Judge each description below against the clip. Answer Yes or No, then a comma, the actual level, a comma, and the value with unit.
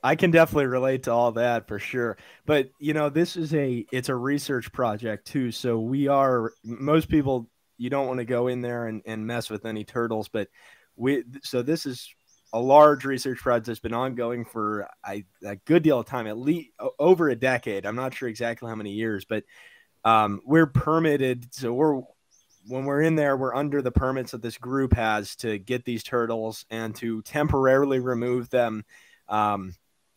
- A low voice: Yes, low, 125 Hz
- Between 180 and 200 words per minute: Yes, average, 195 wpm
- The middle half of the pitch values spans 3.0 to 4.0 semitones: Yes, average, 3.4 semitones